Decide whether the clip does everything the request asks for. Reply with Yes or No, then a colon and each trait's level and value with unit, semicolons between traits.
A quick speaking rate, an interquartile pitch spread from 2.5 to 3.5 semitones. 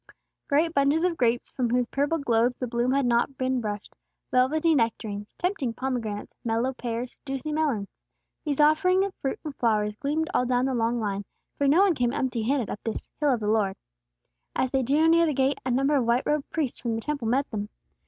No: fast, 210 wpm; average, 4.0 semitones